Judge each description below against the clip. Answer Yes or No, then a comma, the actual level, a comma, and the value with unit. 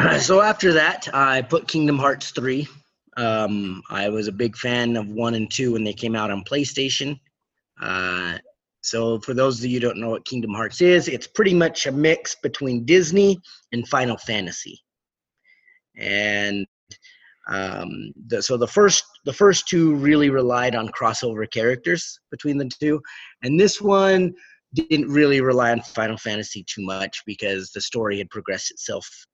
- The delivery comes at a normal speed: Yes, average, 165 wpm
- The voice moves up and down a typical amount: No, wide, 6.0 semitones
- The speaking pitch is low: Yes, low, 125 Hz